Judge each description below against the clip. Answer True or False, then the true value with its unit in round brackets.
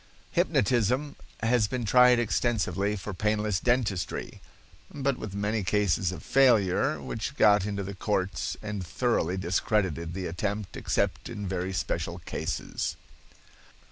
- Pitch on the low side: True (105 Hz)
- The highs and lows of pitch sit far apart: False (3.6 semitones)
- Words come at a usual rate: False (125 wpm)